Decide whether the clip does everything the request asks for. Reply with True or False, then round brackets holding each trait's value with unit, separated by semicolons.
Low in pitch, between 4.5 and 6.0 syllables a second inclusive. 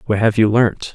True (110 Hz; 5.1 syllables/s)